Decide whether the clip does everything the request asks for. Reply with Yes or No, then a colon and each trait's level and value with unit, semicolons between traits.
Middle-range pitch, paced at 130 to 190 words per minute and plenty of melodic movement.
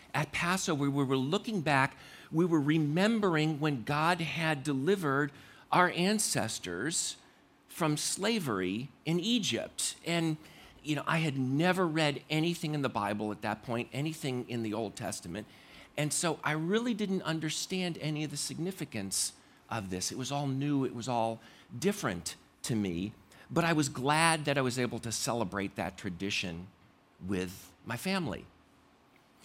Yes: medium, 145 Hz; average, 155 wpm; wide, 6.0 semitones